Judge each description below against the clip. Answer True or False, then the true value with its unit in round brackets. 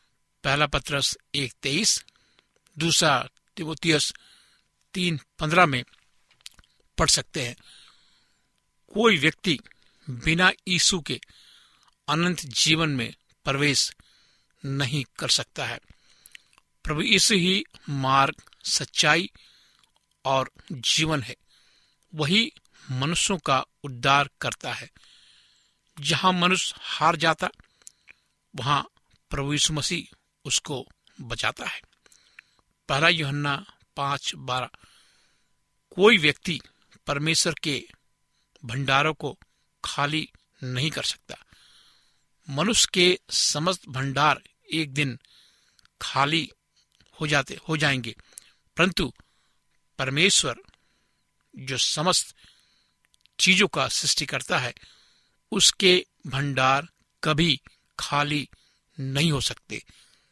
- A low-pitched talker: False (150 Hz)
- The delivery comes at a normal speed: False (90 wpm)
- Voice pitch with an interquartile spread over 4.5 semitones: False (3.6 semitones)